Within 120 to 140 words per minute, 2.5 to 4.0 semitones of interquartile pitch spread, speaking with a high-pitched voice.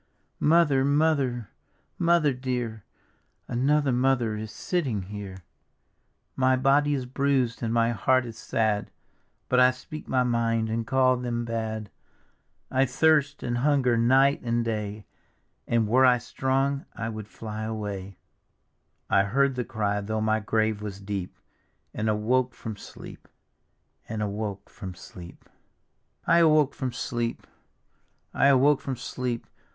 No: slow, 135 wpm; average, 3.5 semitones; low, 120 Hz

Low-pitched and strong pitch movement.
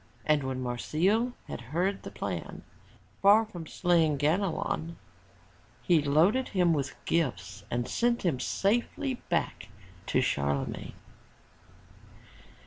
No: medium, 165 Hz; wide, 6.8 semitones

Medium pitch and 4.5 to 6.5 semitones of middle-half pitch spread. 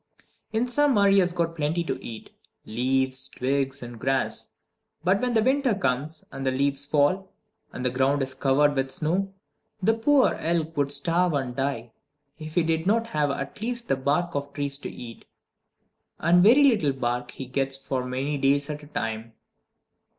Yes: medium, 145 Hz; average, 5.1 semitones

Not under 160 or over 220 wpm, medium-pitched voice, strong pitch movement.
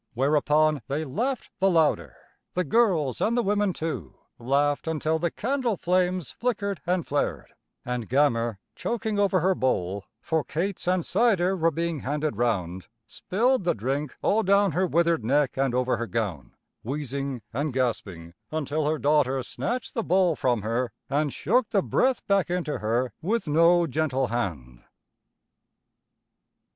No: average, 150 wpm; medium, 155 Hz; wide, 6.5 semitones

